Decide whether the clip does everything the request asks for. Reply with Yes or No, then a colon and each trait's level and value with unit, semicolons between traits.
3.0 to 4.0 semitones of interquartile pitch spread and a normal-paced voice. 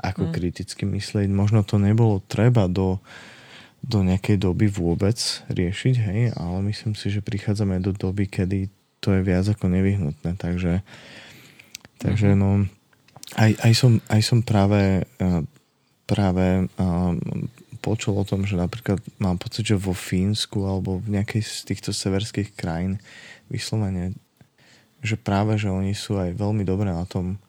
No: narrow, 2.5 semitones; average, 145 wpm